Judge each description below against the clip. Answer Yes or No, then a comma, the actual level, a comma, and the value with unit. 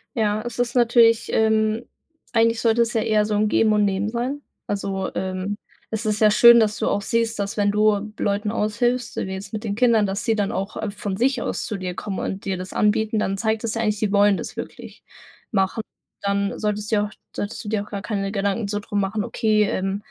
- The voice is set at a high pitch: Yes, high, 210 Hz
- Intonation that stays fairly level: Yes, narrow, 2.0 semitones